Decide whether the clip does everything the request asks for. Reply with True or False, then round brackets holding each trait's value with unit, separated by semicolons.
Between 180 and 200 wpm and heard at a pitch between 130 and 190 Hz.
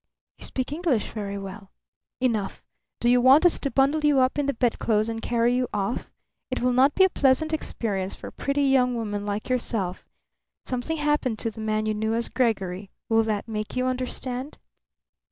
False (190 wpm; 245 Hz)